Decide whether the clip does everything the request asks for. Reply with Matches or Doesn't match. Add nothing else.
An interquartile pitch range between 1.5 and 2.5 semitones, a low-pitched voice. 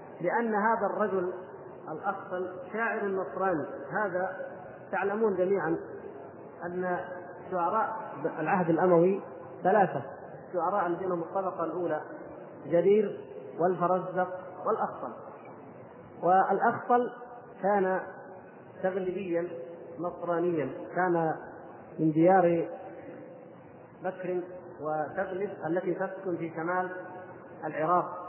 Doesn't match